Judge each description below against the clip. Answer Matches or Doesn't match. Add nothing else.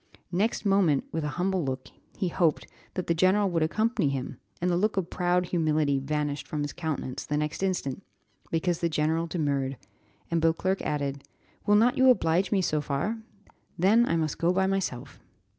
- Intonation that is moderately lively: Matches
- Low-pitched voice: Doesn't match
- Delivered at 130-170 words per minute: Doesn't match